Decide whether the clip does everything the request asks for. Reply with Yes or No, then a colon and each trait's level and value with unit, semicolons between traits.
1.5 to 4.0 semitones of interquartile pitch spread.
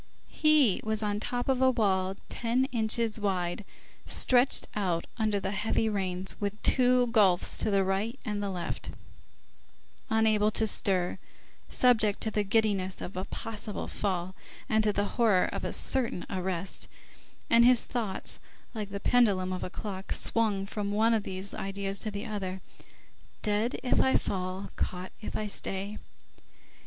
Yes: average, 2.7 semitones